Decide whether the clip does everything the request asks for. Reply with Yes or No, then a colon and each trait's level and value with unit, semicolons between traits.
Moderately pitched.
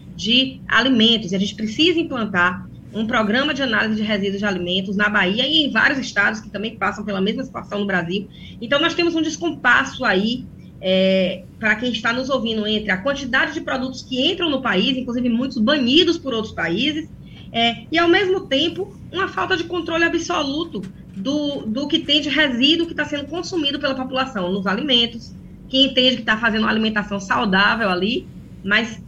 No: high, 240 Hz